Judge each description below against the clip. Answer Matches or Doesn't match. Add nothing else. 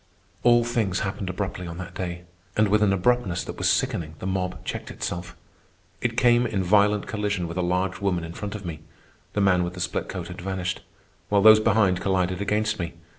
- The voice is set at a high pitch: Doesn't match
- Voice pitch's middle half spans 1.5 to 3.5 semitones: Matches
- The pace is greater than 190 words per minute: Matches